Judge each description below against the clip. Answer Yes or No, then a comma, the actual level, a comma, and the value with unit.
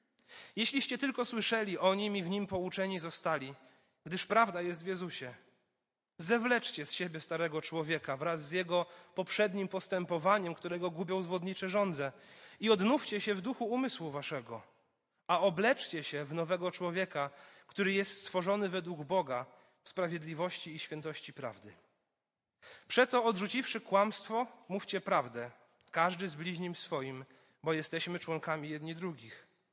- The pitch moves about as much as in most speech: Yes, average, 3.8 semitones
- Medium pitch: Yes, medium, 180 Hz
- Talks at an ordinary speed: Yes, average, 135 wpm